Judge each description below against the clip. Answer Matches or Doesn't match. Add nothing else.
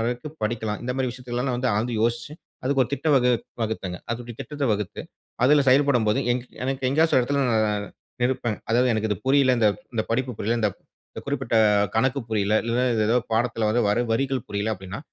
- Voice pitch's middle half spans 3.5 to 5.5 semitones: Doesn't match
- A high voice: Doesn't match